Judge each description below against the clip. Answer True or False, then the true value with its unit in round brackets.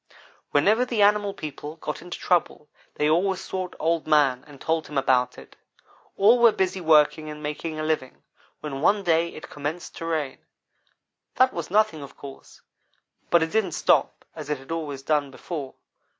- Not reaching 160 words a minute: False (175 wpm)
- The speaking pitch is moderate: True (160 Hz)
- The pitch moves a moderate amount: True (3.8 semitones)